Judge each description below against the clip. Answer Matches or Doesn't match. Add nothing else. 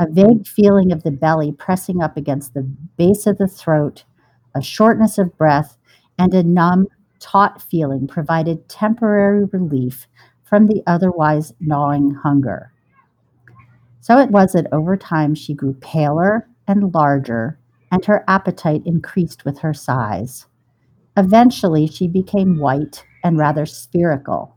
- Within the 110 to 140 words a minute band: Matches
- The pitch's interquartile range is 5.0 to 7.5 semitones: Matches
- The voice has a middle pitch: Matches